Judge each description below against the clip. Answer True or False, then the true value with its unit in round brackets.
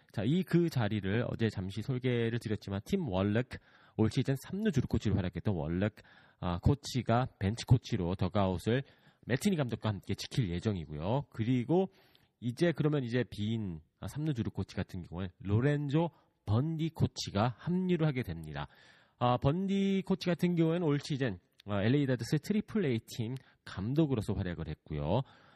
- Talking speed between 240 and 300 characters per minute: False (320 characters per minute)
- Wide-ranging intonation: True (6.4 semitones)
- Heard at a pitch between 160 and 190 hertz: False (120 Hz)